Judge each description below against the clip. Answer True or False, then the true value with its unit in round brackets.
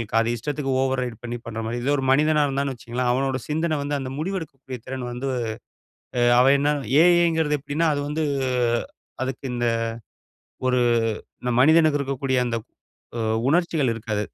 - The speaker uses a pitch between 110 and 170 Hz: True (135 Hz)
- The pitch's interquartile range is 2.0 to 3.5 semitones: True (3.2 semitones)